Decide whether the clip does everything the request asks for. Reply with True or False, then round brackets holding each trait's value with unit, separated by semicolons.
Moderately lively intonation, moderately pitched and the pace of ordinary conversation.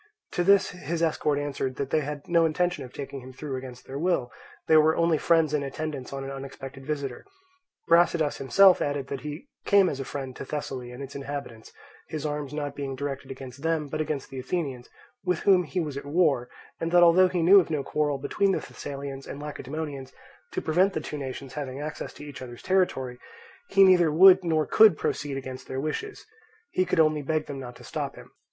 False (3.5 semitones; 145 Hz; 210 wpm)